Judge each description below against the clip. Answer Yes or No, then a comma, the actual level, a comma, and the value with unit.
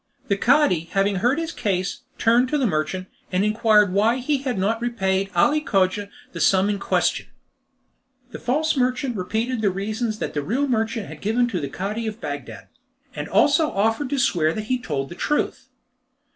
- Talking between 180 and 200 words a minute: Yes, average, 185 wpm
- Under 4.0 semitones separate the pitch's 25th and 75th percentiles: No, average, 4.5 semitones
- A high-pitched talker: Yes, high, 220 Hz